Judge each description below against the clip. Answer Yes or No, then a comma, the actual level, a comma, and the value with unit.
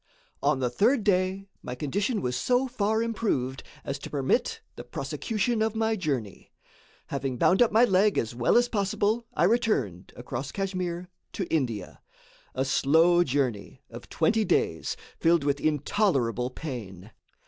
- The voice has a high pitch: No, medium, 170 Hz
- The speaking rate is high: No, average, 150 wpm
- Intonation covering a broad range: Yes, wide, 8.6 semitones